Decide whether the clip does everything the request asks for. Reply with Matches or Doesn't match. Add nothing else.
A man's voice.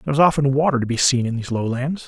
Matches